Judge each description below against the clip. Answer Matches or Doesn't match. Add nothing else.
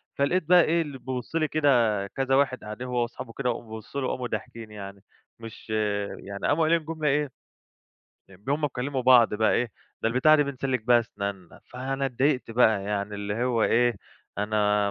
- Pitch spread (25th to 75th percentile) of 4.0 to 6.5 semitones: Matches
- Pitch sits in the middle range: Doesn't match